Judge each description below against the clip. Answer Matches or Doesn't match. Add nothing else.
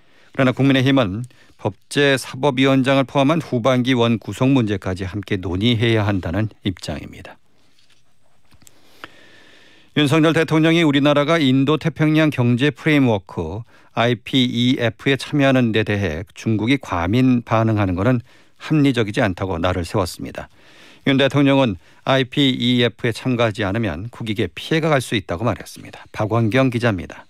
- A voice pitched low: Matches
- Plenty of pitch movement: Doesn't match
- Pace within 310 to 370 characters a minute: Matches